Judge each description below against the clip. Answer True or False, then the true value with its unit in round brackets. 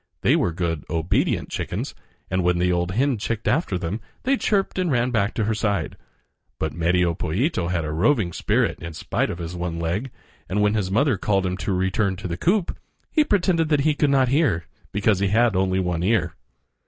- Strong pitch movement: True (6.3 semitones)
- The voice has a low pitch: True (95 Hz)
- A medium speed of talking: False (210 wpm)